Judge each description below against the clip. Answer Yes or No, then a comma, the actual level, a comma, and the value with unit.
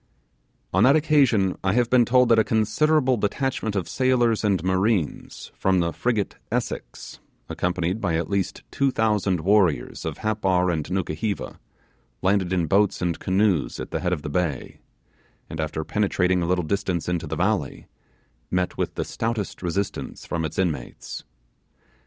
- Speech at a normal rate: Yes, average, 160 wpm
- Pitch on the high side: No, very low, 95 Hz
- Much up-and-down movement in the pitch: No, average, 4.0 semitones